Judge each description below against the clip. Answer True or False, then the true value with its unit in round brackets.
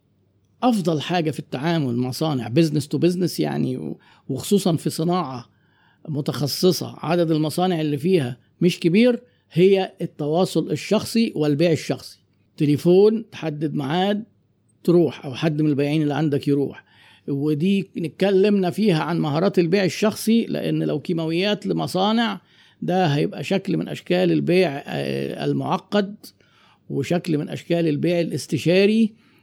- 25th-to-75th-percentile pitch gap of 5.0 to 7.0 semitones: False (4.0 semitones)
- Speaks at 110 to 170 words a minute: True (120 wpm)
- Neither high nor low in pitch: True (165 Hz)